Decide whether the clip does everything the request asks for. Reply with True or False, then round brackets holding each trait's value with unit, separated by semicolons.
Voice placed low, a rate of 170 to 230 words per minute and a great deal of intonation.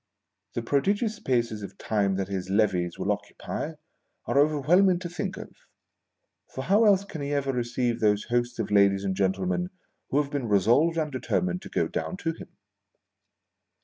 True (130 Hz; 180 wpm; 8.2 semitones)